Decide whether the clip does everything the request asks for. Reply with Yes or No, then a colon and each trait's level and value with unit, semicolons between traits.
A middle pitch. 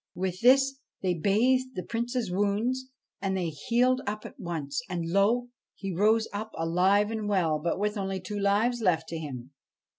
No: high, 200 Hz